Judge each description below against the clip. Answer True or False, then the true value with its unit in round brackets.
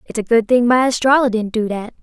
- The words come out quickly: True (265 wpm)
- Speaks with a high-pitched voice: True (235 Hz)